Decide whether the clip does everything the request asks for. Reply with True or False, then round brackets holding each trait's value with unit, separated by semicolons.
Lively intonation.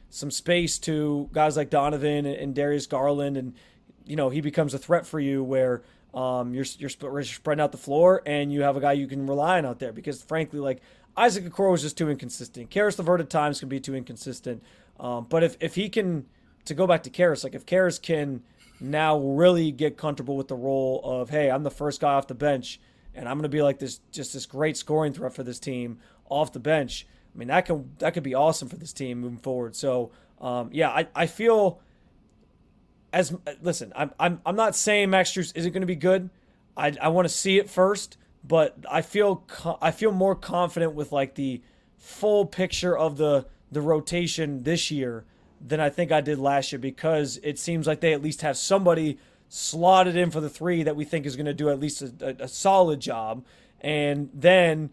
False (3.7 semitones)